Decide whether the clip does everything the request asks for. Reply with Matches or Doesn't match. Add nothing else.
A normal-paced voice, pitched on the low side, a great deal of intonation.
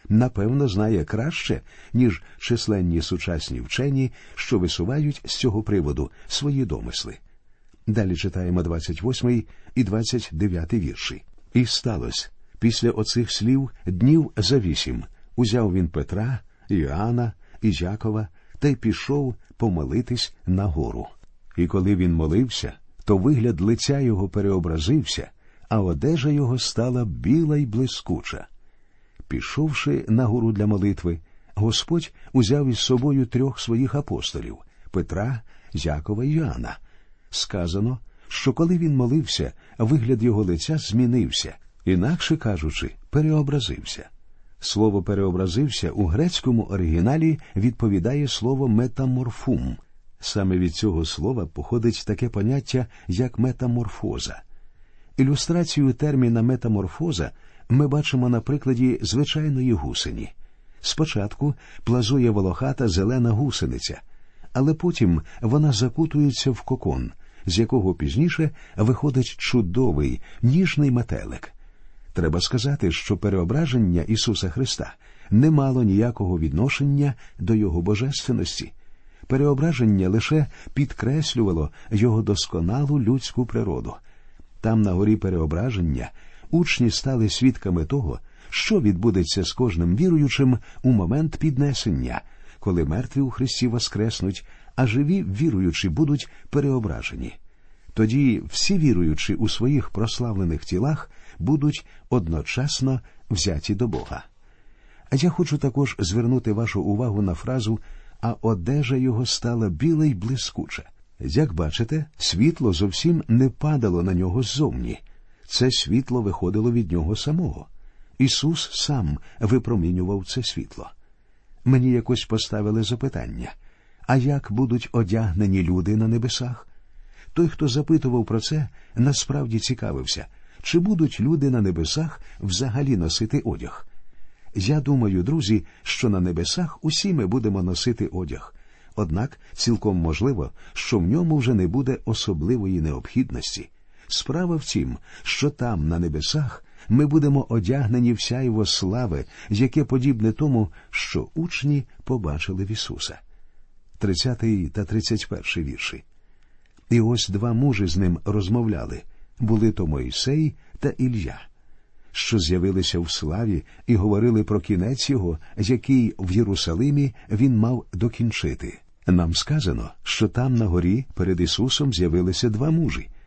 Matches